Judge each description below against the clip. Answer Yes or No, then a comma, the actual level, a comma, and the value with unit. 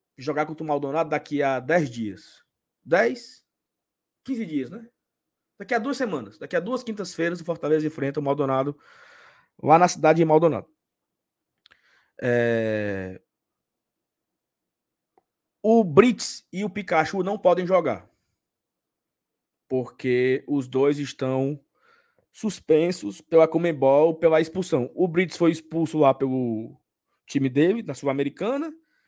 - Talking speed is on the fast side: No, slow, 120 wpm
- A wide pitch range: Yes, wide, 6.4 semitones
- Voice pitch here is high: No, medium, 160 Hz